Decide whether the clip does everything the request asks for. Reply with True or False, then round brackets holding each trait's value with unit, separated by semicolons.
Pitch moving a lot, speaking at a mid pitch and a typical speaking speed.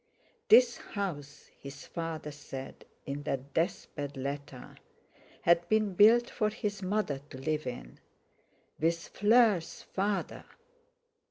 False (6.5 semitones; 165 Hz; 105 wpm)